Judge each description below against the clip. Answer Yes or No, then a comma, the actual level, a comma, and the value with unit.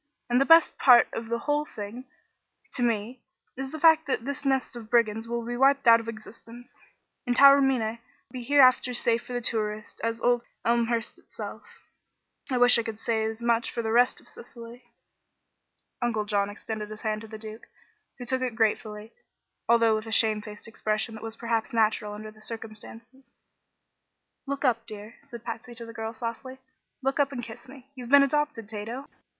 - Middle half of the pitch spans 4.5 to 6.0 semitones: No, narrow, 2.5 semitones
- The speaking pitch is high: Yes, high, 235 Hz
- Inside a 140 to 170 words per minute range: No, average, 185 wpm